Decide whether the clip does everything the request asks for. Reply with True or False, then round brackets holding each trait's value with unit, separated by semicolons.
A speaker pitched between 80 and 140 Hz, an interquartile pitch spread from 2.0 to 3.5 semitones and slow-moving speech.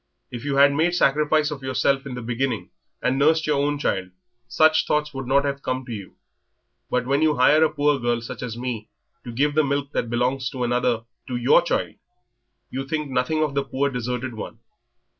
False (135 Hz; 2.9 semitones; 205 wpm)